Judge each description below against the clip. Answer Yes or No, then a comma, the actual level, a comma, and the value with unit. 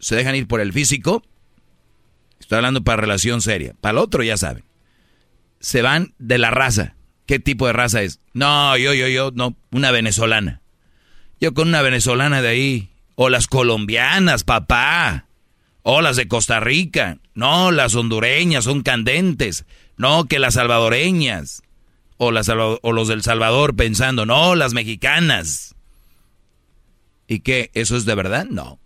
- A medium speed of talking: Yes, average, 155 wpm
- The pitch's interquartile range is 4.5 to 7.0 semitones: No, average, 3.6 semitones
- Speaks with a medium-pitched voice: No, low, 125 Hz